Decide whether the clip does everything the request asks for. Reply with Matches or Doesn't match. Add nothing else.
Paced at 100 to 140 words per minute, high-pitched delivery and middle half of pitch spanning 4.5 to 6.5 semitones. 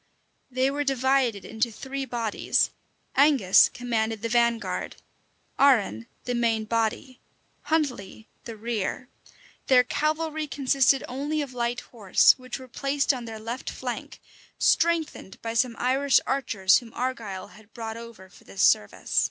Doesn't match